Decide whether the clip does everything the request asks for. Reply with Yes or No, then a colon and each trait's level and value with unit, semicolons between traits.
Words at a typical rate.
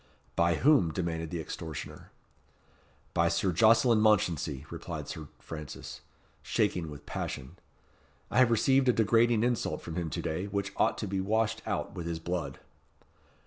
Yes: average, 150 wpm